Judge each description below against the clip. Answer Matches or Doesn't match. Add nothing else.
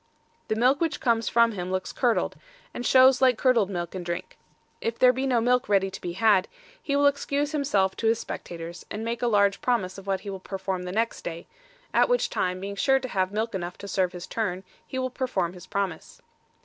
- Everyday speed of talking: Doesn't match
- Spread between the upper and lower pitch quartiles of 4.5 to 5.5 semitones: Matches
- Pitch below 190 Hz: Doesn't match